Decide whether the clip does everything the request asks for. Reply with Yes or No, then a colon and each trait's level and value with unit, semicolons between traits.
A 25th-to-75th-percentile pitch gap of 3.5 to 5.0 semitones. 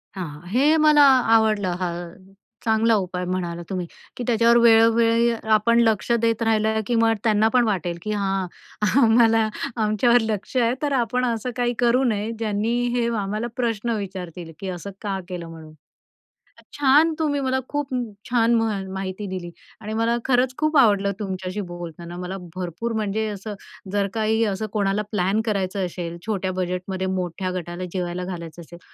Yes: average, 3.9 semitones